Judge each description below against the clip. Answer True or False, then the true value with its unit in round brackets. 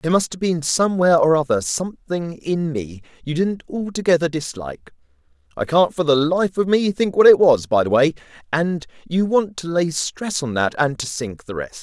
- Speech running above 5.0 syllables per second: True (5.2 syllables/s)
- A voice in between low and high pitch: True (160 Hz)